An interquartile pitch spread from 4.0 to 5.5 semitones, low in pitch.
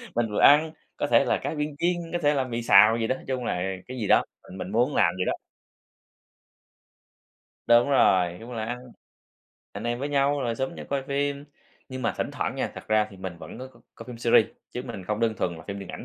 Yes: average, 4.4 semitones; low, 120 Hz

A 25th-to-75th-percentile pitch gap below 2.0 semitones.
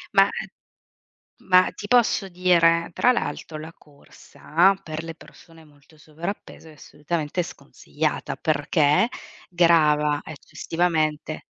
No: narrow, 2.6 semitones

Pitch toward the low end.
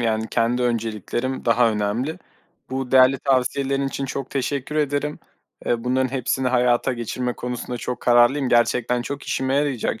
Yes: low, 125 Hz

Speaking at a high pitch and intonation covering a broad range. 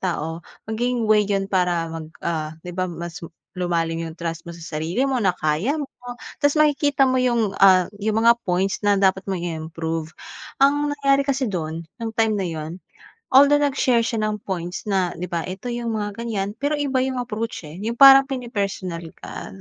Yes: high, 205 Hz; wide, 6.4 semitones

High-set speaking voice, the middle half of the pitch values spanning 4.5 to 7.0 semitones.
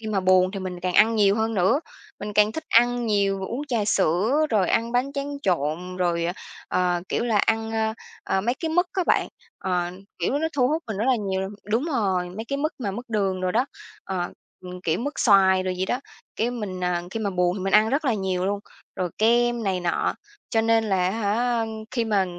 No: high, 210 Hz; average, 4.1 semitones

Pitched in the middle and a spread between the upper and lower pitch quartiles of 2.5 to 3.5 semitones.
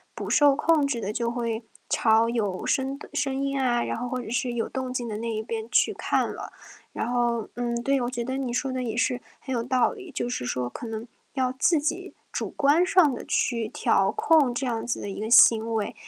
No: high, 245 Hz; average, 2.9 semitones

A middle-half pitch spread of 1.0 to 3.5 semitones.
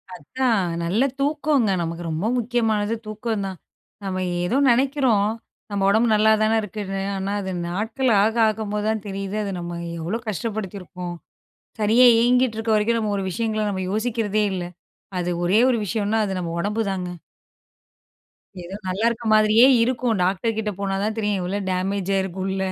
Yes: average, 2.8 semitones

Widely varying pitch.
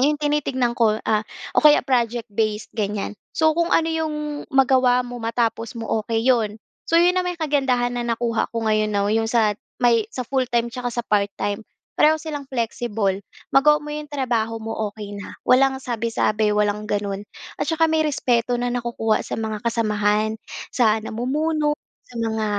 No: average, 3.8 semitones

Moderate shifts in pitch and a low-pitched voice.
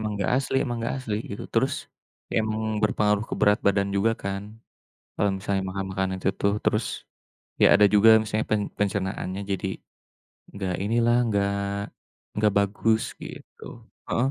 No: narrow, 1.8 semitones; low, 105 Hz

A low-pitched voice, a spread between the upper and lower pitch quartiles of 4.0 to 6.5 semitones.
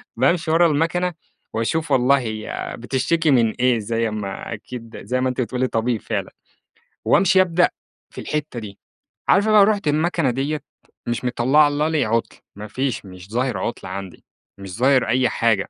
Yes: low, 125 Hz; average, 5.2 semitones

